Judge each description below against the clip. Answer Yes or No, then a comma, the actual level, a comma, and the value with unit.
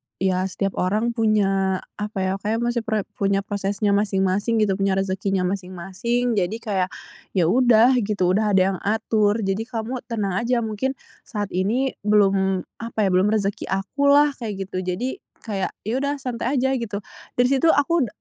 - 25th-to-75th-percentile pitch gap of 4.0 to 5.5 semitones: No, average, 3.4 semitones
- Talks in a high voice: Yes, high, 210 Hz